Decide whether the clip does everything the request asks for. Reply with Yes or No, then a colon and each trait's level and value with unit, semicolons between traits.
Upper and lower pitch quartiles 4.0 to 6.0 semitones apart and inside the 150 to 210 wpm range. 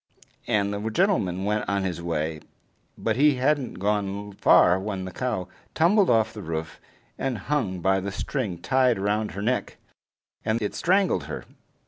Yes: average, 5.0 semitones; average, 160 wpm